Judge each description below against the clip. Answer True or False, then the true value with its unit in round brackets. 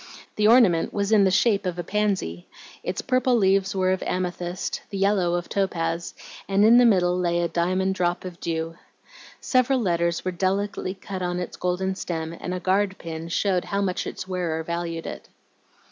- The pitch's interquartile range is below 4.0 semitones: True (2.4 semitones)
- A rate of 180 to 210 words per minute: True (185 wpm)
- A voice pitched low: False (185 Hz)